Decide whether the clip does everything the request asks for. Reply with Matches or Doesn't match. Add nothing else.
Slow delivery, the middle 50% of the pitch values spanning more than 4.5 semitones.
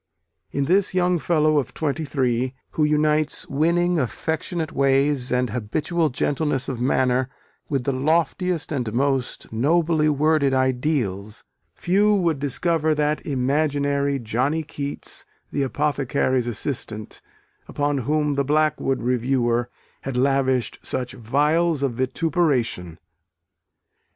Doesn't match